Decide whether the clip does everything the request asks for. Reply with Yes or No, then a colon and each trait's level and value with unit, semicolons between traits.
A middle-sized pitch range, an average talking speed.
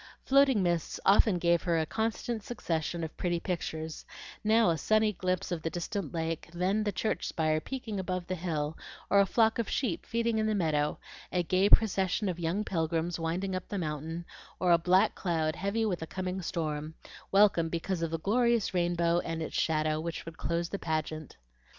Yes: average, 3.6 semitones; average, 190 wpm